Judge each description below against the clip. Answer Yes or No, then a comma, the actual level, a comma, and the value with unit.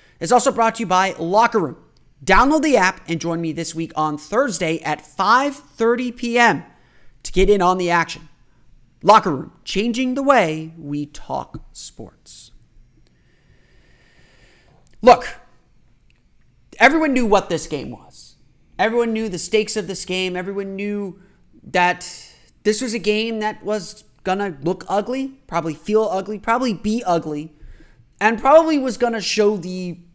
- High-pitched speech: Yes, high, 200 Hz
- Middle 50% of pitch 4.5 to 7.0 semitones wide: Yes, average, 5.2 semitones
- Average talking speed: Yes, average, 150 wpm